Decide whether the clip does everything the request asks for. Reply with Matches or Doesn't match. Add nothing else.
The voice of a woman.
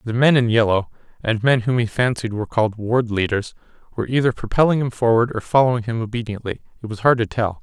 Doesn't match